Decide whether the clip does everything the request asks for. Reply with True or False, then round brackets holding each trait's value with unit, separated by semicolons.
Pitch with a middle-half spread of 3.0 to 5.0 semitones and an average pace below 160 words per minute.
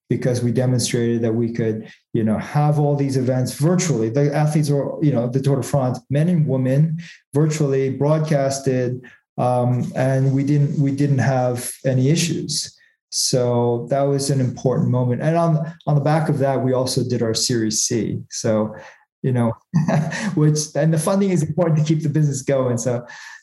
False (3.6 semitones; 180 wpm)